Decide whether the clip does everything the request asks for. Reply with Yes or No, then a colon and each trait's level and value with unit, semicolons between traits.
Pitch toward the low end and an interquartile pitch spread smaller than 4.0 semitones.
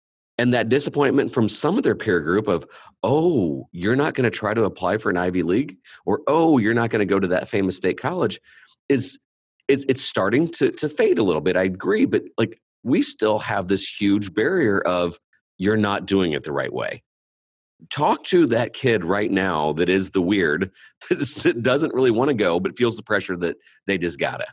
No: low, 100 Hz; average, 4.3 semitones